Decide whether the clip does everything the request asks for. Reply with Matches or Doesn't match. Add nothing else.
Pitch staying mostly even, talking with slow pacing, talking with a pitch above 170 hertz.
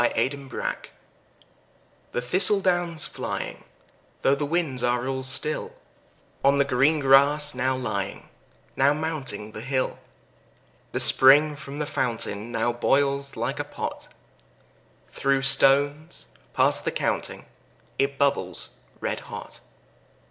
Doesn't match